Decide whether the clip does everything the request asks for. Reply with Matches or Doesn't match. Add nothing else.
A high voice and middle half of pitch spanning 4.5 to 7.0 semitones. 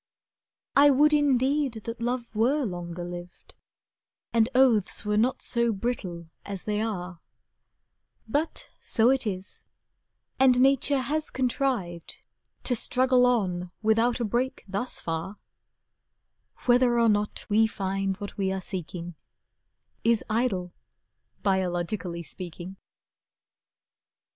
Matches